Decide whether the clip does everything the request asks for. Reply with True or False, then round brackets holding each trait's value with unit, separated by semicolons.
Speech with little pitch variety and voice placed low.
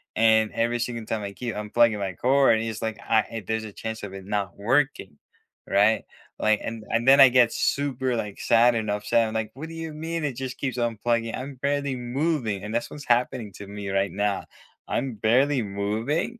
False (3.7 semitones; 115 Hz)